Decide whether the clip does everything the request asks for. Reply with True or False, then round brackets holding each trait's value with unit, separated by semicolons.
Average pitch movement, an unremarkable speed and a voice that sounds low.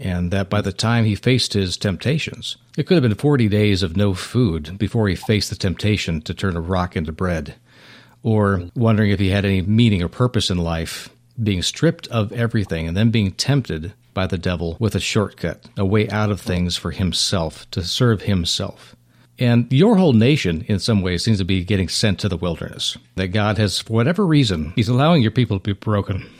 False (3.8 semitones; 210 wpm; 105 Hz)